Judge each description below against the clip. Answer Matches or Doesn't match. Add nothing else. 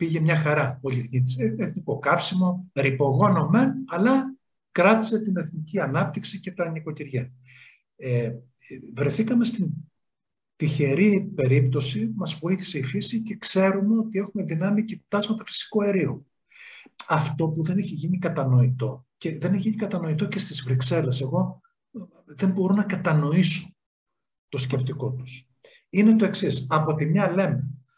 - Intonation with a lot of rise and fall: Matches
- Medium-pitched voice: Matches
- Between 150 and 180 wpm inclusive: Doesn't match